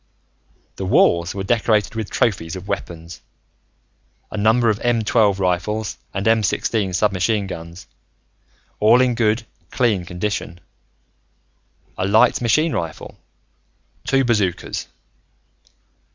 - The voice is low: Yes, low, 105 Hz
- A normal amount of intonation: Yes, average, 3.6 semitones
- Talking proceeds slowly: Yes, slow, 110 wpm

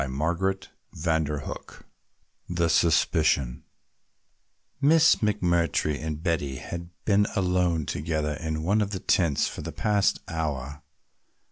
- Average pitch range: Yes, average, 3.4 semitones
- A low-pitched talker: Yes, very low, 80 Hz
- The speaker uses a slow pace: Yes, slow, 115 wpm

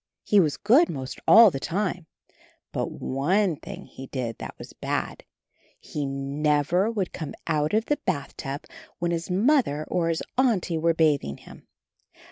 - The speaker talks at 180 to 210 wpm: No, average, 160 wpm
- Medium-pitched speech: Yes, medium, 165 Hz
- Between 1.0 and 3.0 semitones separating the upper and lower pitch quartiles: No, wide, 5.5 semitones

